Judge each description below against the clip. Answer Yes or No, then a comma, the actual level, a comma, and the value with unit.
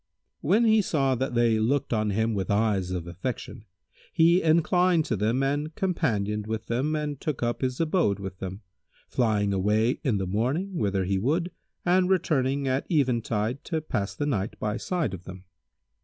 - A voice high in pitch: No, low, 120 Hz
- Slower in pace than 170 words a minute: No, average, 175 wpm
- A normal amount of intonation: No, wide, 6.8 semitones